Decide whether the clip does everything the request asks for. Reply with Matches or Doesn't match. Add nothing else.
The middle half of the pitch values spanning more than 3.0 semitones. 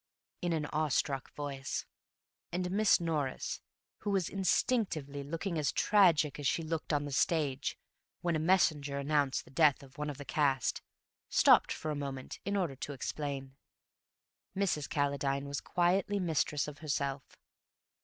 Matches